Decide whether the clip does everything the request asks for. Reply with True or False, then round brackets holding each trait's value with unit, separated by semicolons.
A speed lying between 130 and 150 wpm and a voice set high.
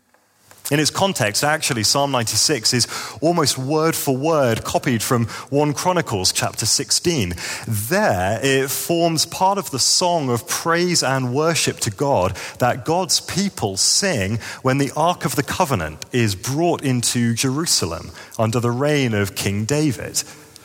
False (145 wpm; 135 Hz)